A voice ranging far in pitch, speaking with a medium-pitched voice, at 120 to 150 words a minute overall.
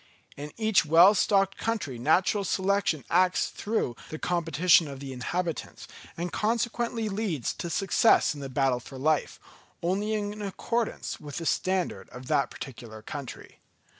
Yes: wide, 6.2 semitones; medium, 175 Hz; average, 145 wpm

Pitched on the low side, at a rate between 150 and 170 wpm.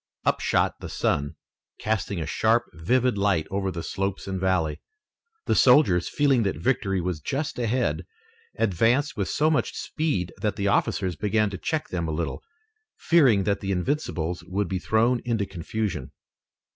Yes: low, 100 Hz; average, 160 wpm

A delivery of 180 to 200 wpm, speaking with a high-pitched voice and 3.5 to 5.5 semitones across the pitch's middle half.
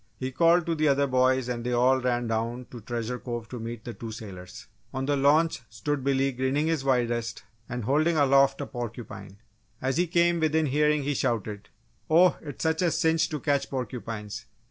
No: average, 190 wpm; low, 130 Hz; average, 4.0 semitones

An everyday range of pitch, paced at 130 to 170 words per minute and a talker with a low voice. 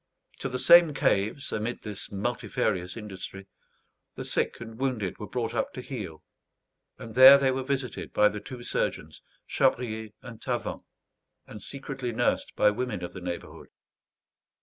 Yes: average, 3.9 semitones; average, 150 wpm; low, 115 Hz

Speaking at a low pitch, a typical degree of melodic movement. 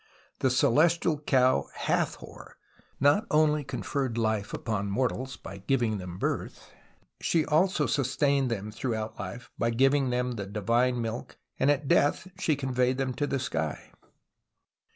Yes: low, 130 Hz; average, 4.0 semitones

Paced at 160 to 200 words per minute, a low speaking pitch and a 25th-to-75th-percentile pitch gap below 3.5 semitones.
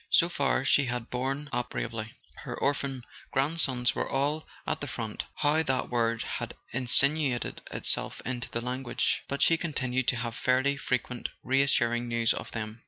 Yes: average, 170 wpm; low, 130 Hz; narrow, 2.6 semitones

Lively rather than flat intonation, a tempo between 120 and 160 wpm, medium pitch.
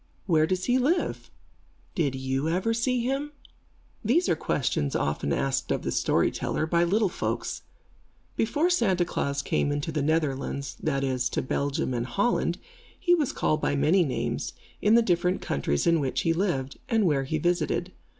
No: wide, 7.4 semitones; average, 170 wpm; medium, 165 Hz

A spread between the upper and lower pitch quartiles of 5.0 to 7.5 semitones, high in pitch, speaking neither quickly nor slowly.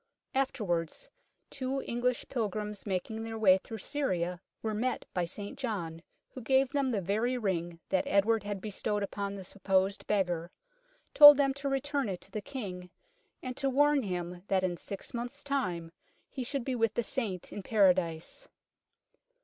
Yes: wide, 5.6 semitones; high, 210 Hz; average, 165 wpm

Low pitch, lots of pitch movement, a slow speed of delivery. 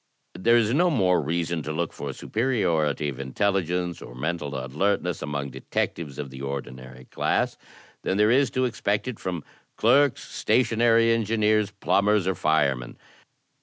No: very low, 90 Hz; wide, 7.0 semitones; average, 155 wpm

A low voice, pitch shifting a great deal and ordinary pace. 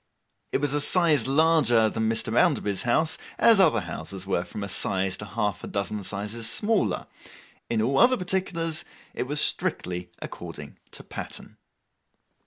Yes: low, 115 Hz; wide, 8.0 semitones; average, 155 wpm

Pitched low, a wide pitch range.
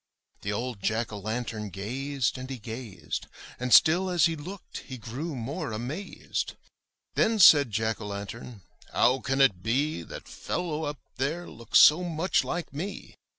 Yes: low, 130 Hz; wide, 5.9 semitones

